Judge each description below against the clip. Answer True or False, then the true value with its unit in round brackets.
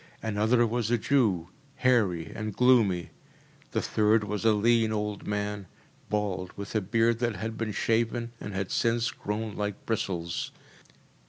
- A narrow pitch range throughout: True (2.1 semitones)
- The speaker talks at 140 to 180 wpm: True (150 wpm)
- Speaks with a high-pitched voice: False (110 Hz)